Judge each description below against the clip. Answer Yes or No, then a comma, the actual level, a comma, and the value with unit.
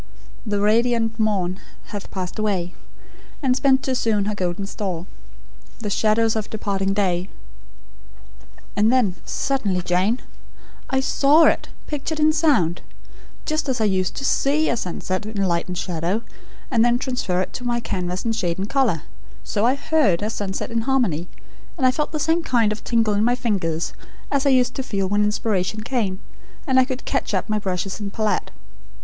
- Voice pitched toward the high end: Yes, high, 215 Hz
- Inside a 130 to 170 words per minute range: No, average, 180 wpm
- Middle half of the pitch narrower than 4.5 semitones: No, average, 5.1 semitones